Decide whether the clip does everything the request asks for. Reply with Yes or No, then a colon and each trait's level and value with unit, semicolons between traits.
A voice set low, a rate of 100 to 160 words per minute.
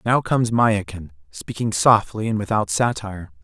Yes: low, 105 Hz; average, 140 wpm